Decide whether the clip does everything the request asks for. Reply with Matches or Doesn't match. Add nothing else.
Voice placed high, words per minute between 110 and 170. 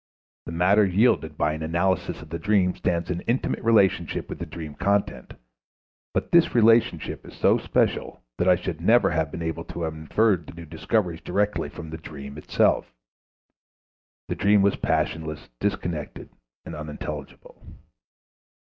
Doesn't match